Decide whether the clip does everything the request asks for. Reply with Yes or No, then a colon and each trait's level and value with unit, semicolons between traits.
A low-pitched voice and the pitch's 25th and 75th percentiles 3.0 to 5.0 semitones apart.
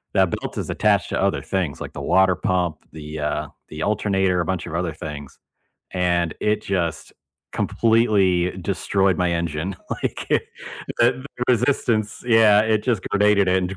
Yes: very low, 95 Hz; average, 3.5 semitones